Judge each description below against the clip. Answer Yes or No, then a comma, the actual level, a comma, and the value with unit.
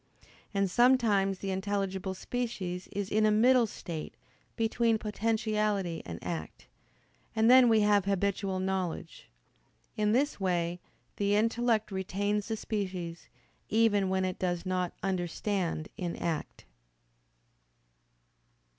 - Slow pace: Yes, slow, 115 wpm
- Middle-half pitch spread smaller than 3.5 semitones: Yes, average, 2.9 semitones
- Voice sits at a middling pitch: No, high, 200 Hz